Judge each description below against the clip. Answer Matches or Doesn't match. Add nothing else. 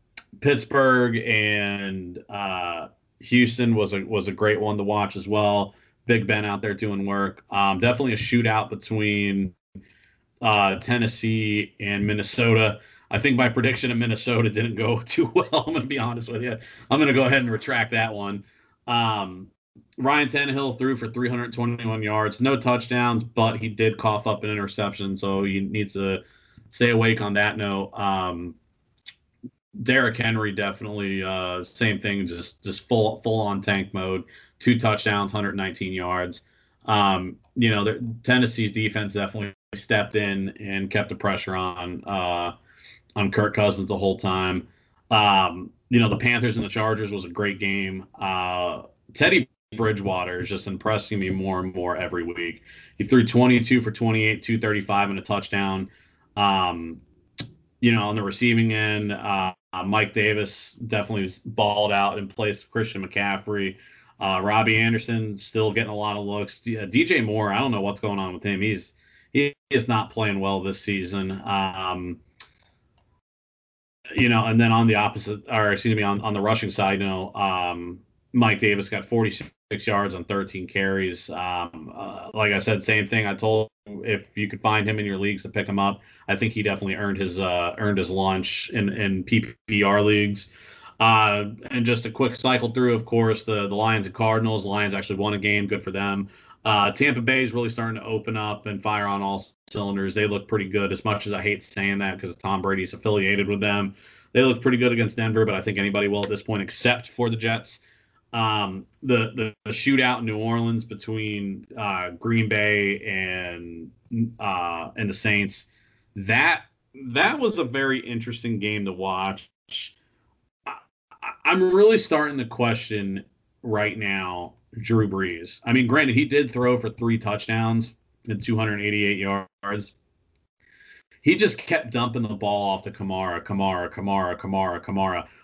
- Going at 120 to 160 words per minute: Doesn't match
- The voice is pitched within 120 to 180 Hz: Doesn't match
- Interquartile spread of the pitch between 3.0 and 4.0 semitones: Doesn't match